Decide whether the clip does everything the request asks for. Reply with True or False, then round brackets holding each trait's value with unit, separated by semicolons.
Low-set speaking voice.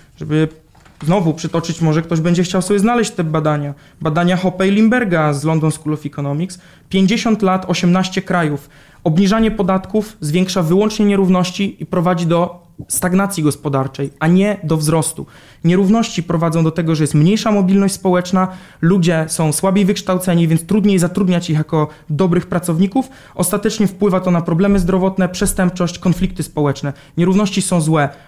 False (180 Hz)